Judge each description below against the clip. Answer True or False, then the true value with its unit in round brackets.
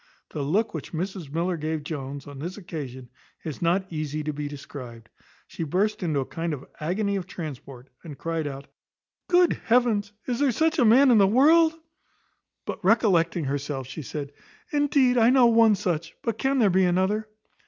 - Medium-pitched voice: True (175 Hz)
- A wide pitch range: True (7.2 semitones)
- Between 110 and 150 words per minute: False (180 wpm)